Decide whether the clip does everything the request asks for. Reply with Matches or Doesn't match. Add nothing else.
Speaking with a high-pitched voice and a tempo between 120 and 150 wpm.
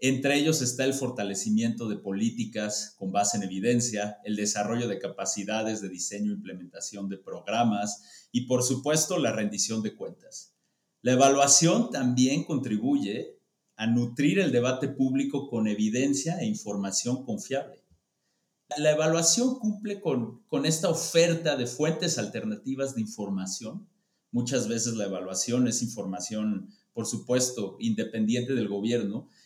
Doesn't match